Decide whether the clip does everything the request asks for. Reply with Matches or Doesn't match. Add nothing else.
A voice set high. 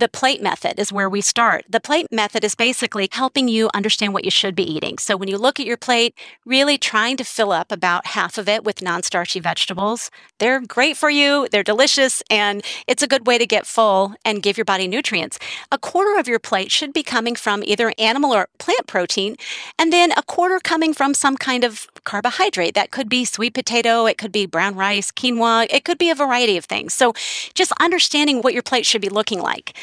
Matches